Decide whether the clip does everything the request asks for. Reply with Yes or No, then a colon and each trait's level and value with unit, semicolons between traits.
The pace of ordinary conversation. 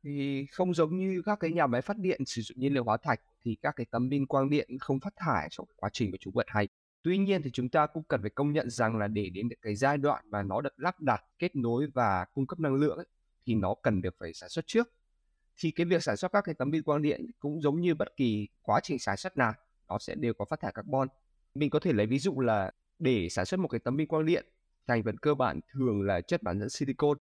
No: fast, 275 wpm